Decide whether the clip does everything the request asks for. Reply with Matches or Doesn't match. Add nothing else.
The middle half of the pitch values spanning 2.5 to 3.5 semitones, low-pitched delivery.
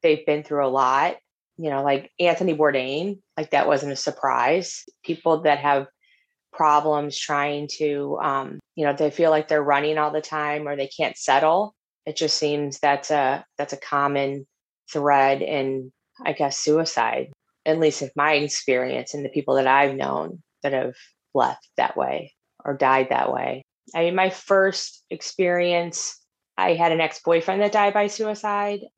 Doesn't match